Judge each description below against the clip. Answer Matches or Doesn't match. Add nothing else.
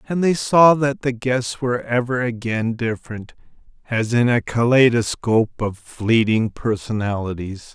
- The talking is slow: Matches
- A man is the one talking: Matches